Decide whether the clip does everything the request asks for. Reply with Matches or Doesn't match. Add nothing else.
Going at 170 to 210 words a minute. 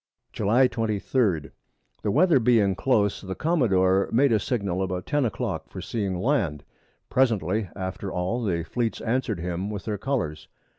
Doesn't match